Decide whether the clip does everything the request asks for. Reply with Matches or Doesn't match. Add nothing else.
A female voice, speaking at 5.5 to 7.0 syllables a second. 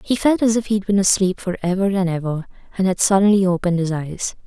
Matches